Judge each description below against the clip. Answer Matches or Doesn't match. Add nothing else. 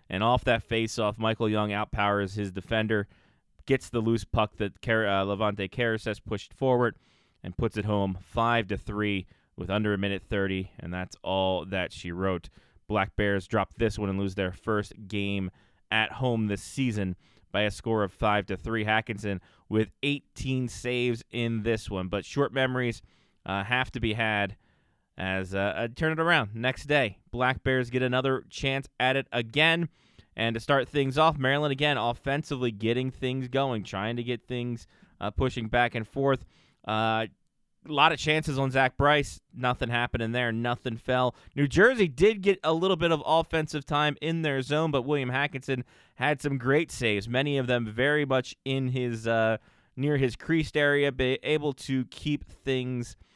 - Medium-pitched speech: Doesn't match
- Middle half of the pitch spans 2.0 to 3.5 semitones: Doesn't match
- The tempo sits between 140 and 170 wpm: Doesn't match